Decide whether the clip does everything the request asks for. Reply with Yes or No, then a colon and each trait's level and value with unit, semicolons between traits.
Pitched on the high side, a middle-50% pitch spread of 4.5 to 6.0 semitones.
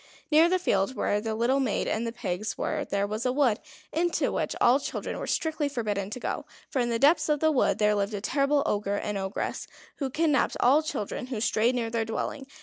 Yes: high, 240 Hz; average, 5.2 semitones